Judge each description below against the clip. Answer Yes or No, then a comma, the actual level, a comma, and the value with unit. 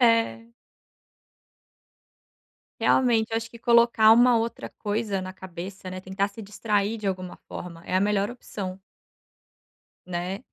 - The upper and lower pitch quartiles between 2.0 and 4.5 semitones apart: Yes, average, 3.4 semitones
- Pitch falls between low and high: No, high, 205 Hz